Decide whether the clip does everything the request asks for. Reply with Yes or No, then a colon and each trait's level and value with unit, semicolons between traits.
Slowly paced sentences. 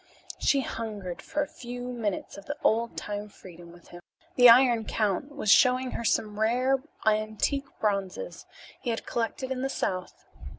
No: average, 165 wpm